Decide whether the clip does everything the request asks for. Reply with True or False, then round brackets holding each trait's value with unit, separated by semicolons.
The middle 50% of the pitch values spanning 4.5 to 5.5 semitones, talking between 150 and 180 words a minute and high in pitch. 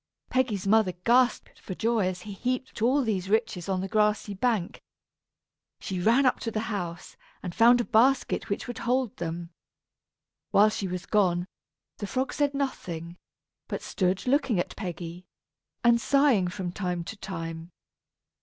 True (5.0 semitones; 155 wpm; 205 Hz)